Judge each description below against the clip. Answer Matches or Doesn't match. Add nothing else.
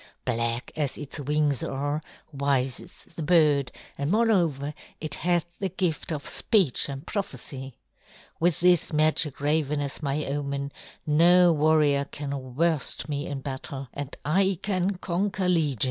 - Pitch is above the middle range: Doesn't match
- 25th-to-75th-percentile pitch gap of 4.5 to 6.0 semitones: Doesn't match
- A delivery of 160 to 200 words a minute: Doesn't match